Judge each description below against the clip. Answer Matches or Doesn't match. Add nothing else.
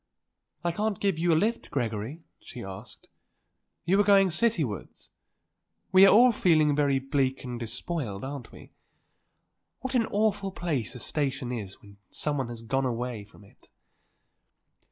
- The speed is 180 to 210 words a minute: Doesn't match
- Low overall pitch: Doesn't match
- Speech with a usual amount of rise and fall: Doesn't match